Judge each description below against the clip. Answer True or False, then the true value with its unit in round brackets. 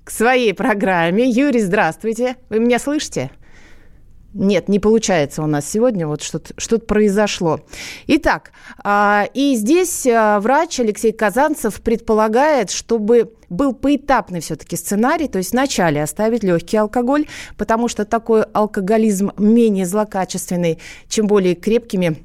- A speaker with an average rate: True (120 wpm)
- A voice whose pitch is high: True (215 Hz)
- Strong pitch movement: False (4.2 semitones)